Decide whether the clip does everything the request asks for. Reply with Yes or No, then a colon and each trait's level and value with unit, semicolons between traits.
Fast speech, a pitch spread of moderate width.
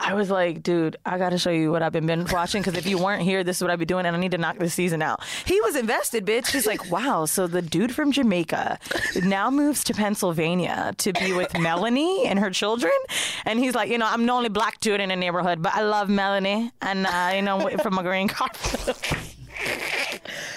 Yes: fast, 230 wpm; average, 3.7 semitones